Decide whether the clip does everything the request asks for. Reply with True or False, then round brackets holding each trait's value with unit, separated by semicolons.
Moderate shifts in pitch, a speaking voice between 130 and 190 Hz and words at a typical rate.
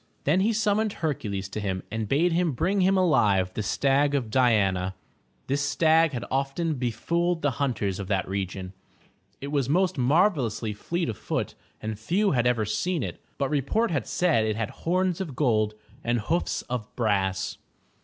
False (7.8 semitones; 135 Hz; 175 wpm)